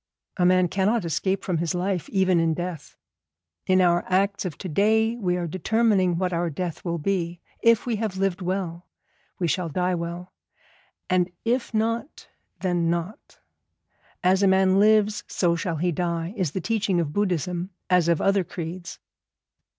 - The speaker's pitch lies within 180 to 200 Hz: Yes, medium, 185 Hz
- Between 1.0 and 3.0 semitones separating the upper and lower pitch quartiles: Yes, narrow, 2.4 semitones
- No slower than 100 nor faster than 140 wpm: No, average, 165 wpm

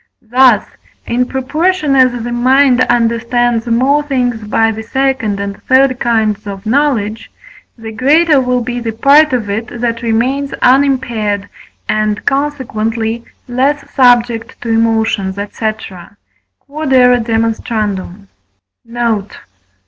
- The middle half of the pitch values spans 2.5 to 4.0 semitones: Yes, average, 2.9 semitones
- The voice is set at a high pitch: Yes, high, 235 Hz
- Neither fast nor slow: No, slow, 110 wpm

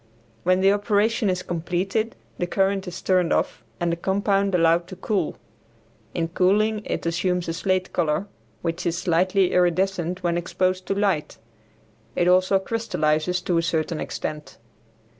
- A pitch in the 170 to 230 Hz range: Yes, medium, 185 Hz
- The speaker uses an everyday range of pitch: No, narrow, 2.3 semitones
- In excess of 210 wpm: No, average, 150 wpm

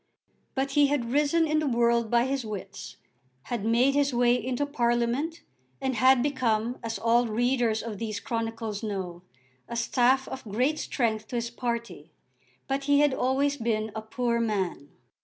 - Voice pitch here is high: Yes, high, 240 Hz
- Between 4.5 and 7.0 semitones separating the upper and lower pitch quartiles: No, average, 3.0 semitones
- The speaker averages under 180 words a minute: Yes, average, 165 wpm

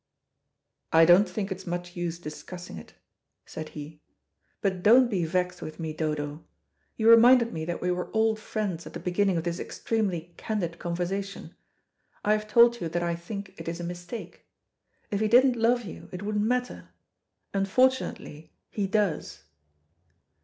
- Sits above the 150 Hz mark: Yes, medium, 185 Hz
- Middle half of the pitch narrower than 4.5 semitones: Yes, average, 4.1 semitones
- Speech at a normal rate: Yes, average, 160 wpm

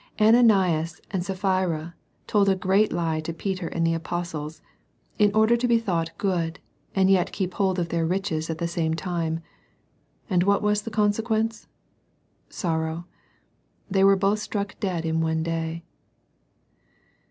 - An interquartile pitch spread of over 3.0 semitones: Yes, average, 3.6 semitones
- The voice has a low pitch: No, medium, 180 Hz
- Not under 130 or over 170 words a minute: Yes, average, 150 wpm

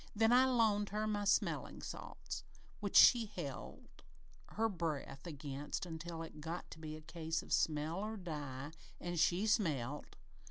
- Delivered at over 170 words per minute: No, average, 155 wpm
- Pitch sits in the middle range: Yes, medium, 170 Hz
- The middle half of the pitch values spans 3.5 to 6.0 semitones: Yes, average, 5.3 semitones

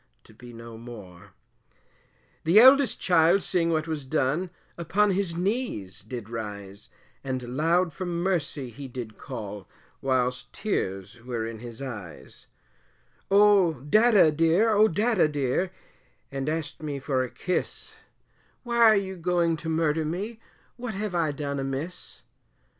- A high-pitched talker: No, medium, 155 Hz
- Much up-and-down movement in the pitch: Yes, wide, 7.1 semitones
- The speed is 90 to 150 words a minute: Yes, average, 140 wpm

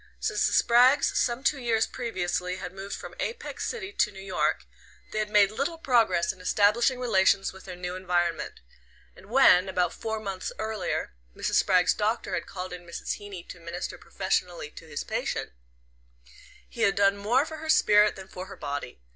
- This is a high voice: Yes, high, 200 Hz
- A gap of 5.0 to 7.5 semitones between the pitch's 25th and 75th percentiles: No, average, 4.3 semitones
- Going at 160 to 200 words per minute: Yes, average, 180 wpm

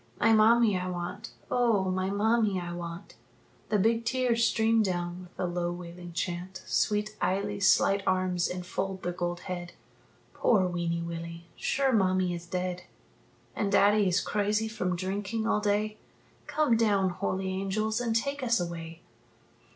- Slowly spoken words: No, average, 150 wpm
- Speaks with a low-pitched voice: No, high, 190 Hz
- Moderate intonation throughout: Yes, average, 3.5 semitones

